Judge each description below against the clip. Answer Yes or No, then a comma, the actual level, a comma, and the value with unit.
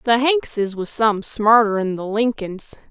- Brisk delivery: No, average, 145 wpm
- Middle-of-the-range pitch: No, high, 220 Hz